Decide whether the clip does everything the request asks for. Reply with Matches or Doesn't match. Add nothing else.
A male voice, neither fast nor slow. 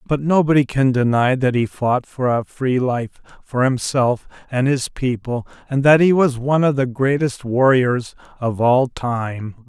Matches